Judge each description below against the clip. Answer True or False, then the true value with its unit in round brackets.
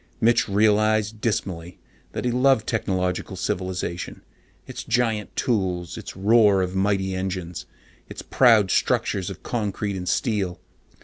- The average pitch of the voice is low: True (100 Hz)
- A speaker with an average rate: False (125 wpm)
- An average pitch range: True (3.1 semitones)